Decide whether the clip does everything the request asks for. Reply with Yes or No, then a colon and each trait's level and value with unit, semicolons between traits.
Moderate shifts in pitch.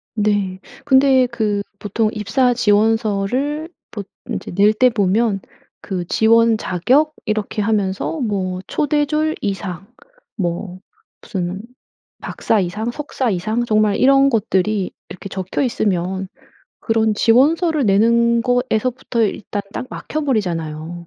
Yes: average, 4.1 semitones